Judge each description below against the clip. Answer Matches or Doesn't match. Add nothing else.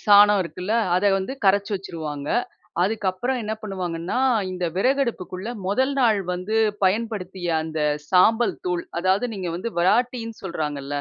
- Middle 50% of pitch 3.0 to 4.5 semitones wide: Matches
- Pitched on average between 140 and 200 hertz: Matches